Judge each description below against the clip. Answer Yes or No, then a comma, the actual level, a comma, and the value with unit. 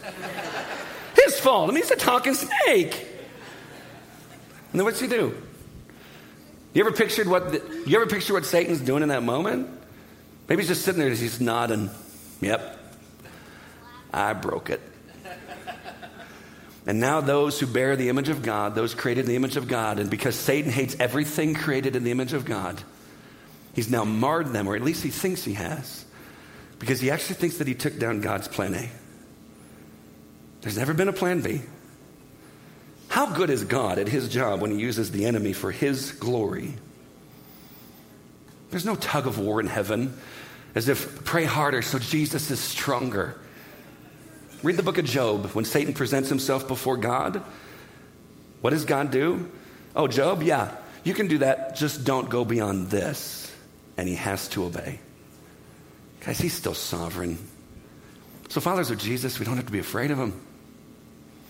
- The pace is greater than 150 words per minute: Yes, average, 170 wpm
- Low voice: Yes, low, 125 Hz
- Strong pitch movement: Yes, wide, 5.7 semitones